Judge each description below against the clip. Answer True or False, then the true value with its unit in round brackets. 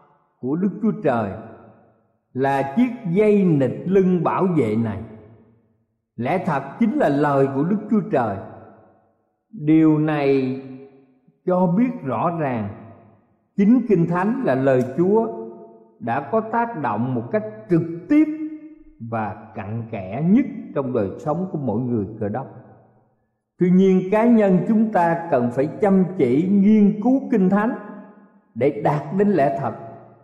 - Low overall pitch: False (145 Hz)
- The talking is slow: True (145 wpm)